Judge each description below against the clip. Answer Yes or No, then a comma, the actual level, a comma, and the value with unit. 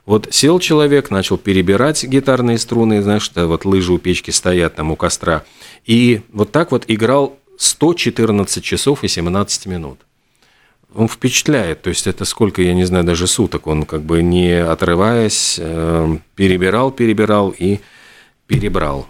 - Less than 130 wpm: No, average, 150 wpm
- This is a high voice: No, low, 100 Hz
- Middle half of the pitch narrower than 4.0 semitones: No, average, 5.0 semitones